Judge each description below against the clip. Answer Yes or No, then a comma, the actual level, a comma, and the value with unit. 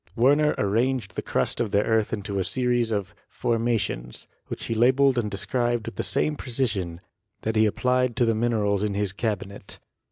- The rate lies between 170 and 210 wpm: Yes, average, 190 wpm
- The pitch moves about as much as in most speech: Yes, average, 3.2 semitones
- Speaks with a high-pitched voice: No, low, 110 Hz